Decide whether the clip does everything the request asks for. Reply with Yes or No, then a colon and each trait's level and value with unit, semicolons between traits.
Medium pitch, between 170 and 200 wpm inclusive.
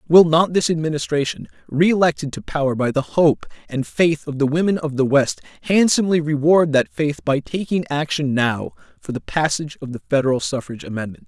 Yes: medium, 150 Hz; average, 180 wpm